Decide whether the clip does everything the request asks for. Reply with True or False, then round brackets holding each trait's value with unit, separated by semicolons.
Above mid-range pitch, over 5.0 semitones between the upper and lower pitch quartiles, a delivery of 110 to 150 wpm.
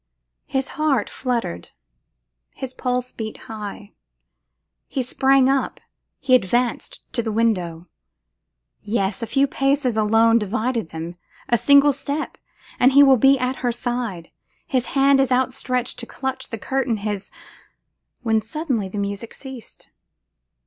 False (245 Hz; 3.6 semitones; 135 wpm)